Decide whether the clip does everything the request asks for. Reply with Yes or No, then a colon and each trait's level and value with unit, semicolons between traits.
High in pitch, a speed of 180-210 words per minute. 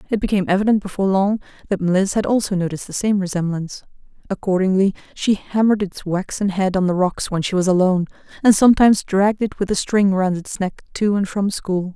Yes: high, 195 Hz; average, 200 wpm